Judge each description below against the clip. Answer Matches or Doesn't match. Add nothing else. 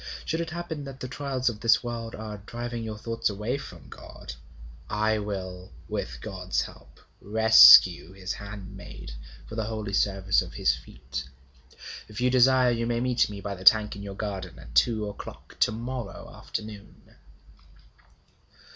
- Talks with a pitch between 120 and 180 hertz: Doesn't match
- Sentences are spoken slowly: Doesn't match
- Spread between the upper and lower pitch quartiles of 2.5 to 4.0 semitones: Matches